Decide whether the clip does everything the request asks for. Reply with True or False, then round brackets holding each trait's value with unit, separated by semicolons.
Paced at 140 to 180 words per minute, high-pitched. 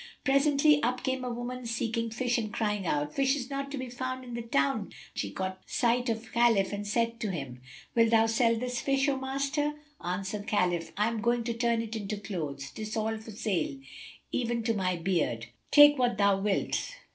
False (200 wpm; 230 Hz)